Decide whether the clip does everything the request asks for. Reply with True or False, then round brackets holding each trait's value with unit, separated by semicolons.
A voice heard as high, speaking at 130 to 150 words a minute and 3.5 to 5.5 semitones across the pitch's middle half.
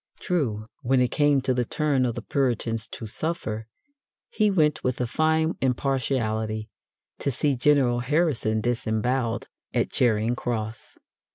False (125 Hz; 140 wpm; 4.3 semitones)